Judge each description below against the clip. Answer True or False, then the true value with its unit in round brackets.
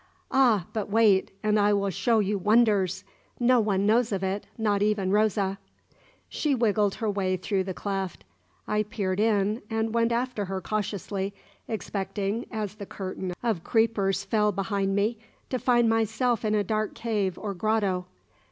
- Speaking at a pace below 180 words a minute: True (160 wpm)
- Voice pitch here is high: True (210 Hz)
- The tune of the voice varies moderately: False (2.3 semitones)